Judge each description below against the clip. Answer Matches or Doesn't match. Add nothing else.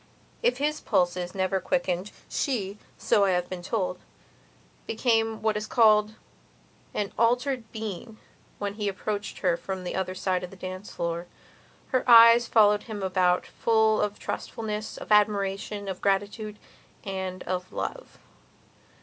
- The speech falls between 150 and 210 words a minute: Doesn't match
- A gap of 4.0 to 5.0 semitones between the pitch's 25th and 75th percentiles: Doesn't match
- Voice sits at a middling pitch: Doesn't match